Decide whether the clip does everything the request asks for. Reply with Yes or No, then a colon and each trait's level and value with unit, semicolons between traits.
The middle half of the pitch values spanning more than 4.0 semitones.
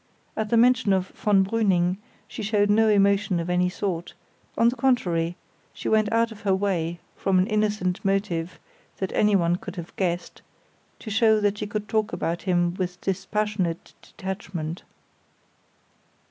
No: average, 3.1 semitones